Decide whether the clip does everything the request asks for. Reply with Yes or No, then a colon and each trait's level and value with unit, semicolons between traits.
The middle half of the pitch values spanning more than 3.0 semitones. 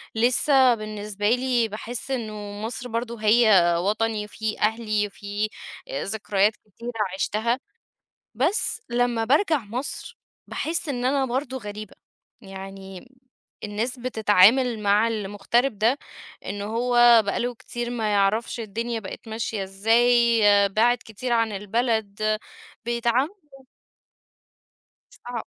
No: narrow, 2.6 semitones